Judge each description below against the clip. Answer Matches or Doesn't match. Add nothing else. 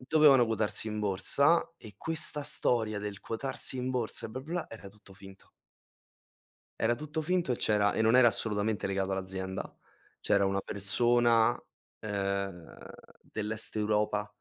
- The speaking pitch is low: Matches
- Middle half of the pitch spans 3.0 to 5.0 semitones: Matches